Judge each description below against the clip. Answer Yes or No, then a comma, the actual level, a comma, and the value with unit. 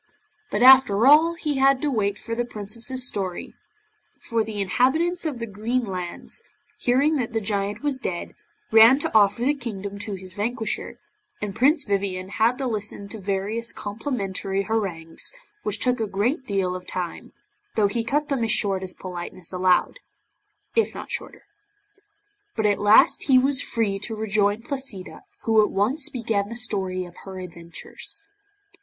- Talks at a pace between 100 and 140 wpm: No, average, 165 wpm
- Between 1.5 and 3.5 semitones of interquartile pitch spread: No, average, 4.3 semitones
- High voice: Yes, high, 215 Hz